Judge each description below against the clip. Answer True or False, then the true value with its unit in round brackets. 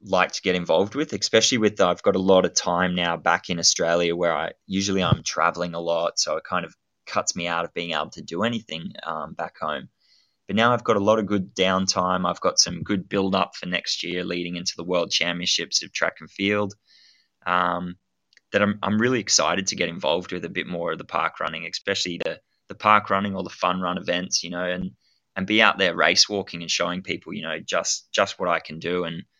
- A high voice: False (90 Hz)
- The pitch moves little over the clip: True (2.1 semitones)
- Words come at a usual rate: False (235 wpm)